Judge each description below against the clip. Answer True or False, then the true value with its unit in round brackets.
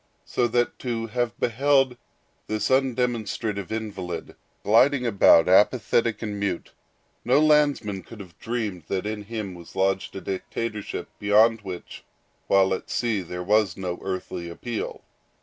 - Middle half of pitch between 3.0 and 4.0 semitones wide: True (3.7 semitones)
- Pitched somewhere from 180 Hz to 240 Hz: False (105 Hz)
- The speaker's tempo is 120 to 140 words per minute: True (135 wpm)